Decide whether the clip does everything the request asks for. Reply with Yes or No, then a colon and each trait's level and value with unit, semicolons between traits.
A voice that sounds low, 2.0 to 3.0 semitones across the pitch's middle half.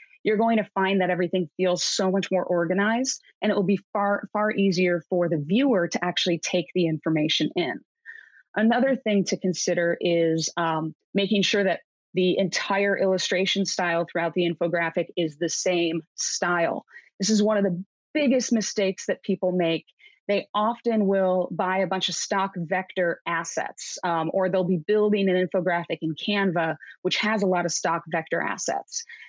No: medium, 185 Hz; average, 2.7 semitones